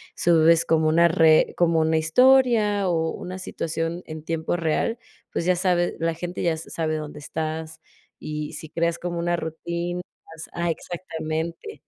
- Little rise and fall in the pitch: Yes, narrow, 1.6 semitones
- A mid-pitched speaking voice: Yes, medium, 165 Hz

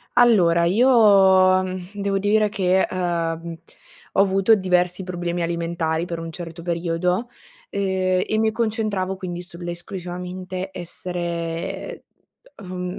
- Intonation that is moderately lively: No, narrow, 2.2 semitones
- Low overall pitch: No, medium, 185 Hz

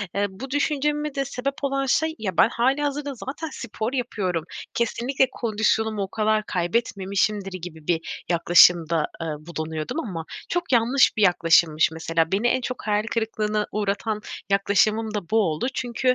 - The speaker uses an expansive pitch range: Yes, wide, 6.1 semitones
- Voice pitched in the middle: No, high, 215 Hz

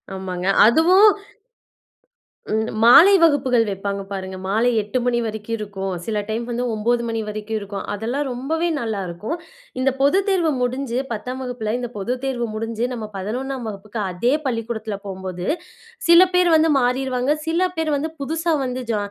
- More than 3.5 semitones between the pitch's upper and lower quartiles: Yes, average, 4.2 semitones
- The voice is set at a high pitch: Yes, high, 235 Hz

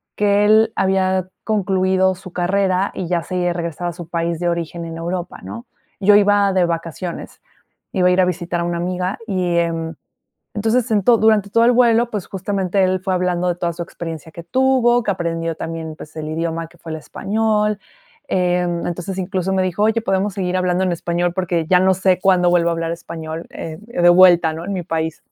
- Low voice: No, medium, 180 Hz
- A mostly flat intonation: Yes, narrow, 2.3 semitones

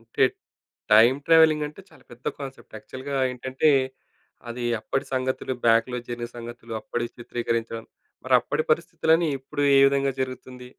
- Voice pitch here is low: Yes, low, 130 Hz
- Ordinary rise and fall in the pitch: Yes, average, 3.1 semitones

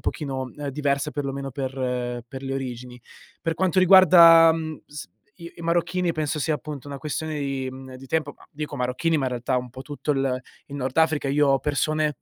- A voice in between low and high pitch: Yes, medium, 145 Hz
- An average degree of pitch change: Yes, average, 3.1 semitones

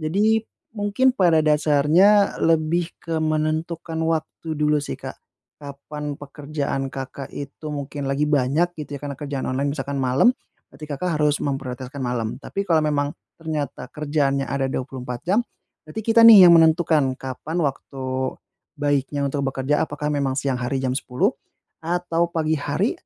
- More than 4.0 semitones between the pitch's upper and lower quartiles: No, average, 2.9 semitones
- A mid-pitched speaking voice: Yes, medium, 150 Hz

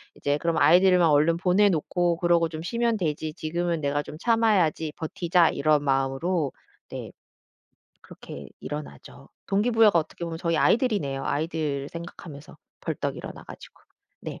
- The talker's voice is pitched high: No, medium, 165 Hz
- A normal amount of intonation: Yes, average, 3.2 semitones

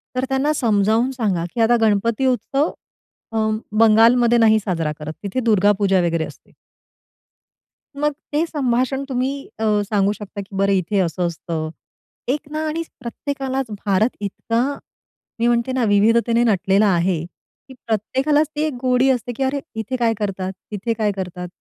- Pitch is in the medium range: No, high, 225 Hz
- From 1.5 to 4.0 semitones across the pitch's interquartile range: No, average, 4.7 semitones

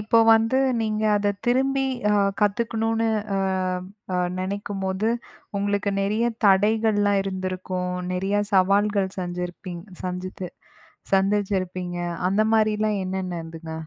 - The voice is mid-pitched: No, high, 200 Hz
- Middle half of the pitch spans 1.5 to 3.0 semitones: Yes, narrow, 2.5 semitones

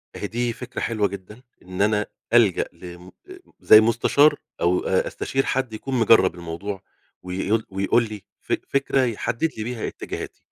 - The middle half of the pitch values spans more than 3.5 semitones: Yes, average, 4.1 semitones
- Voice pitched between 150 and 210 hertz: No, low, 110 Hz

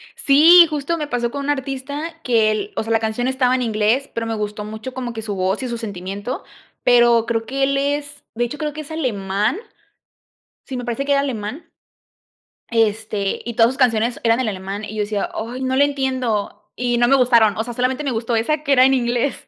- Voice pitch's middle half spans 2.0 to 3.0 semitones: No, average, 3.8 semitones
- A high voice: Yes, high, 240 Hz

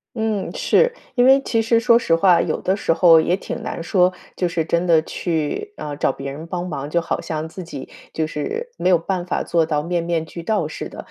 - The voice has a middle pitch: Yes, medium, 170 Hz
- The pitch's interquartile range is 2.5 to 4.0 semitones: Yes, average, 3.5 semitones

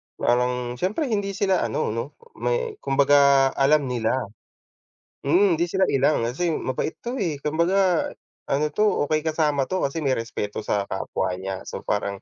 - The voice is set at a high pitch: No, medium, 145 Hz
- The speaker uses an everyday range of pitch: No, wide, 6.6 semitones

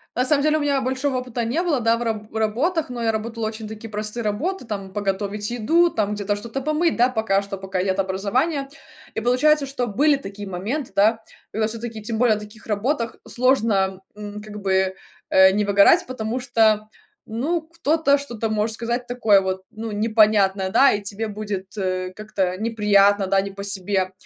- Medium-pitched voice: No, high, 220 Hz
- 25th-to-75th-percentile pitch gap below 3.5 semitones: No, average, 3.8 semitones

